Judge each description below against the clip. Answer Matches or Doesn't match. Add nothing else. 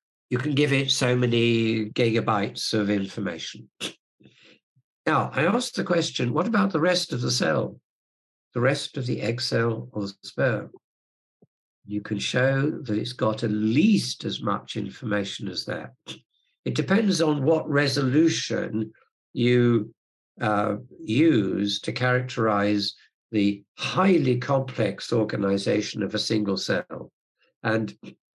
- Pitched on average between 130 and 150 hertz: Doesn't match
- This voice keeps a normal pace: Doesn't match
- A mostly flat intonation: Doesn't match